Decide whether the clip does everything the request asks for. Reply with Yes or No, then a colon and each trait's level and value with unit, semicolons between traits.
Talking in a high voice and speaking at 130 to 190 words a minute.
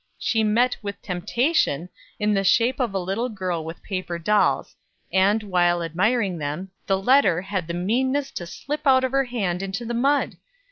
Yes: high, 200 Hz; average, 180 wpm